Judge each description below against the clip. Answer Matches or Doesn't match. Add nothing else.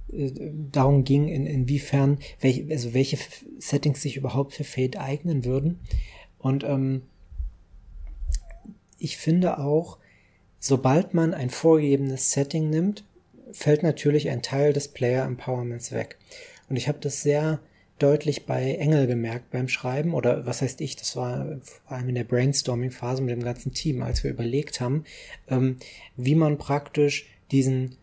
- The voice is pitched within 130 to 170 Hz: Matches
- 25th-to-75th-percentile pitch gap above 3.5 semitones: Doesn't match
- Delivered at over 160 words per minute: Doesn't match